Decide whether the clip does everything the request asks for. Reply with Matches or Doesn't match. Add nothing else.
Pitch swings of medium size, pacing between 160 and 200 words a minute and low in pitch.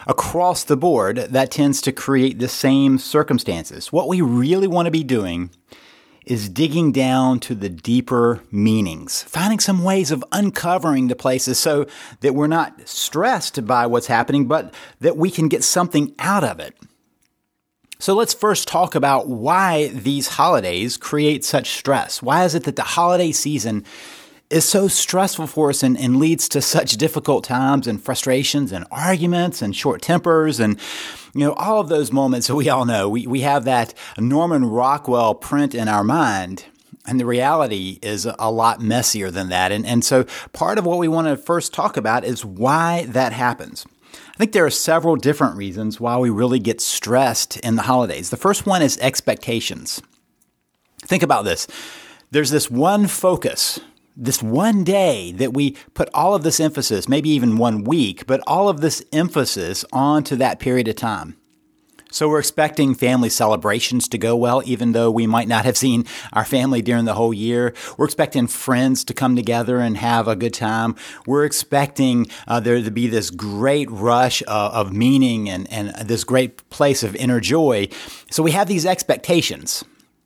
Matches